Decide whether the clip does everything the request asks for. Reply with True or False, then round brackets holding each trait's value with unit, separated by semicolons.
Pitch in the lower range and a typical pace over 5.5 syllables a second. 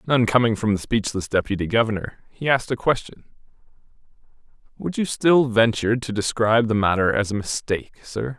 True (115 Hz; 5.8 syllables/s)